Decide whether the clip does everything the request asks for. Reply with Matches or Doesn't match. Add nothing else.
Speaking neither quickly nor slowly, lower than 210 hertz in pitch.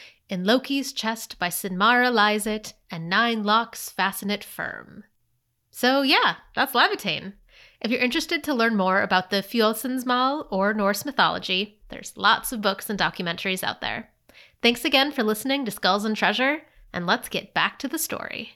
Doesn't match